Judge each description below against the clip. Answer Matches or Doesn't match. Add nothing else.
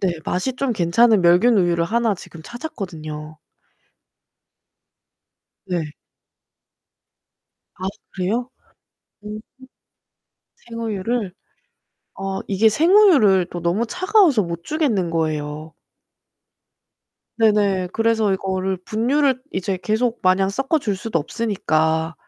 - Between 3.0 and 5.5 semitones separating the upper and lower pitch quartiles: Matches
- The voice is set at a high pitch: Matches